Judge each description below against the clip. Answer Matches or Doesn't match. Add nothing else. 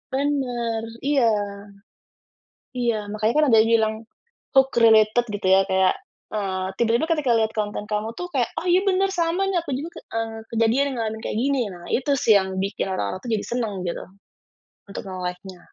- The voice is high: Matches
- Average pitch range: Matches